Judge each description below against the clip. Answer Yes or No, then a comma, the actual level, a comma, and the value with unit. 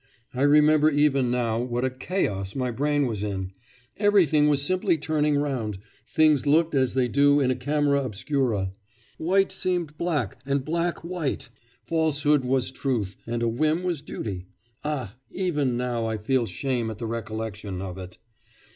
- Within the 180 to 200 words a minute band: No, average, 160 wpm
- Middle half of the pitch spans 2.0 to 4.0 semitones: No, average, 4.6 semitones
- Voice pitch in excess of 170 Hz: No, low, 135 Hz